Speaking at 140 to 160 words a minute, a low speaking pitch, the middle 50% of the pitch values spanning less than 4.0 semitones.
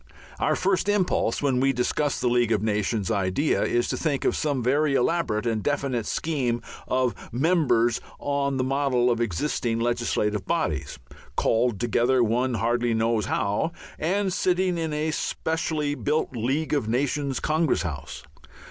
No: average, 150 wpm; low, 130 Hz; average, 4.5 semitones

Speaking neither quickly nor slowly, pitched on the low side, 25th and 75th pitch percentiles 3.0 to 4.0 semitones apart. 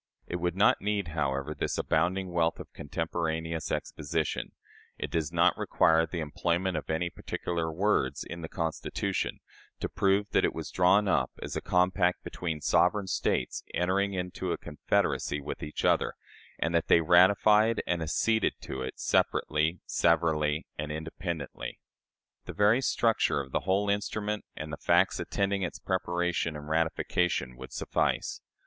Yes: average, 155 wpm; very low, 85 Hz; average, 3.3 semitones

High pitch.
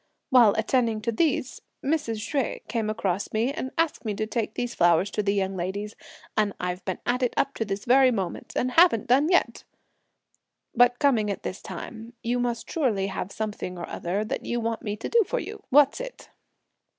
Yes: high, 225 Hz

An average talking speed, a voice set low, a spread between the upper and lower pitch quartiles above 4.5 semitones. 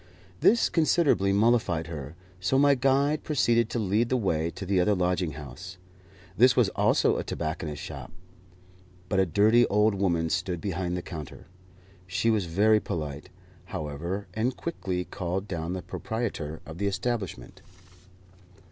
Yes: average, 145 wpm; very low, 95 Hz; average, 5.2 semitones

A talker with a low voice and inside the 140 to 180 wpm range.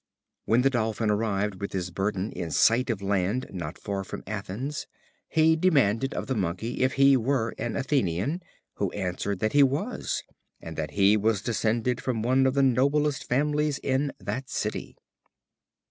Yes: low, 115 Hz; average, 165 wpm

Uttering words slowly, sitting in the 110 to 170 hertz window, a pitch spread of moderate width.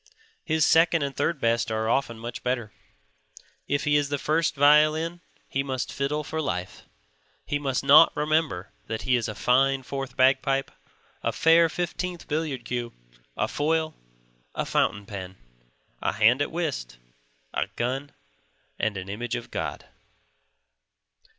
No: average, 145 wpm; medium, 140 Hz; average, 4.5 semitones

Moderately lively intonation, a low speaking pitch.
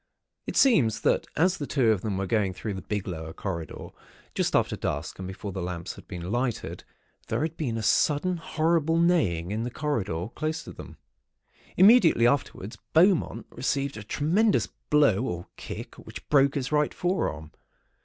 No: wide, 8.7 semitones; low, 120 Hz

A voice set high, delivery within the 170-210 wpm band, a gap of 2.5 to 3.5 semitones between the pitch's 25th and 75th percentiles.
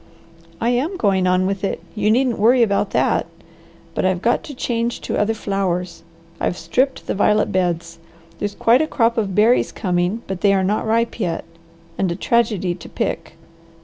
No: high, 205 Hz; average, 180 wpm; average, 4.0 semitones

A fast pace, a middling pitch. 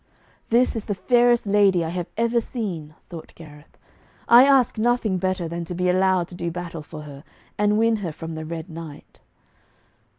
No: average, 185 wpm; medium, 180 Hz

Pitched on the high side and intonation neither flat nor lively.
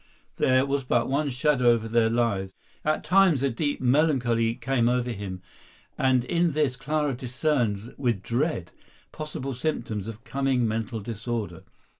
No: low, 125 Hz; average, 3.5 semitones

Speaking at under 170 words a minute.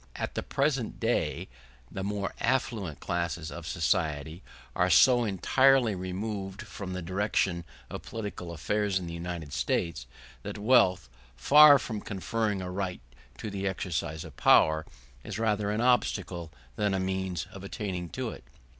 Yes: average, 150 wpm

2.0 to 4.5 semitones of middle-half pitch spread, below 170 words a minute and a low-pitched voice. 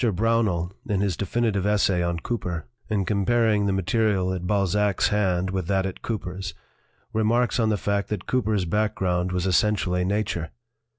Yes: average, 2.8 semitones; average, 155 wpm; low, 100 Hz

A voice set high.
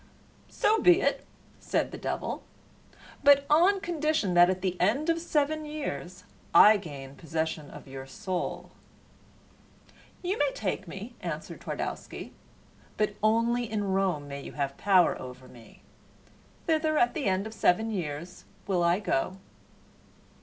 Yes: high, 195 Hz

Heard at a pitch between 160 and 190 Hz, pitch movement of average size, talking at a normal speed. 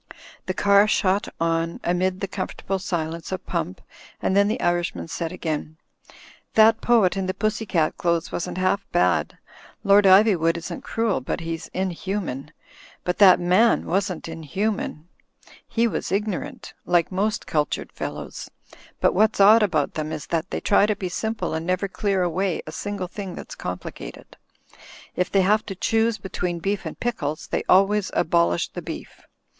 Yes: medium, 185 Hz; average, 3.3 semitones; average, 165 wpm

